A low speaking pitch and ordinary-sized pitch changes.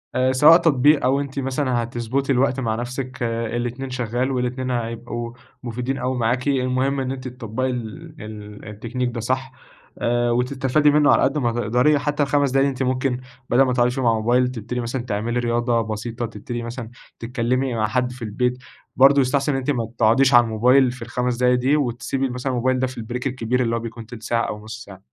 No: low, 125 Hz; narrow, 2.1 semitones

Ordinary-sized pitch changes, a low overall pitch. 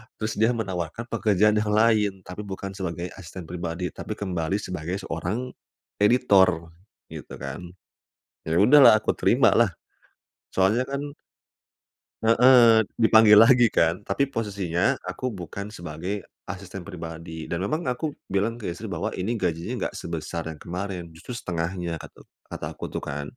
Yes: average, 4.3 semitones; very low, 95 Hz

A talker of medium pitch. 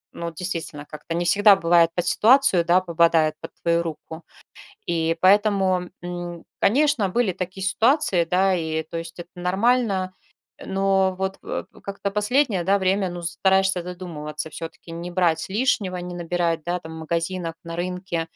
Yes: medium, 180 Hz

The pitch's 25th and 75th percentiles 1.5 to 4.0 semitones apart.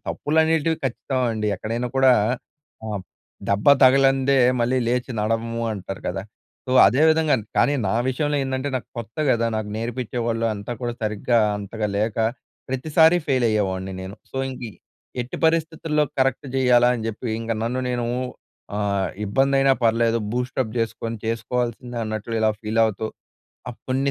Yes: average, 3.3 semitones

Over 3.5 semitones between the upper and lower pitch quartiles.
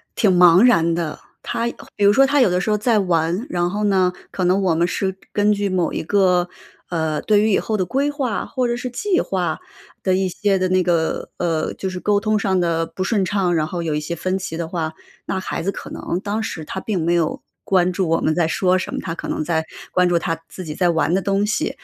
No: average, 3.2 semitones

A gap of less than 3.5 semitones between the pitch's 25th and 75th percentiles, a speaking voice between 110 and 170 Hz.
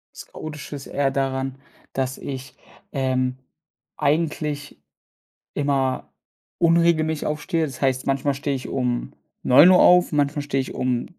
Yes: narrow, 2.5 semitones; medium, 140 Hz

